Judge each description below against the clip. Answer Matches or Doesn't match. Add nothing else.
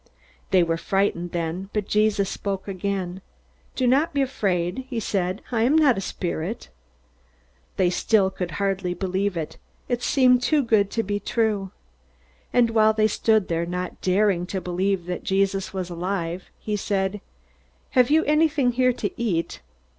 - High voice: Matches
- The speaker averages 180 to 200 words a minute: Doesn't match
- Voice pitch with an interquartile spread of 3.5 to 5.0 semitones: Matches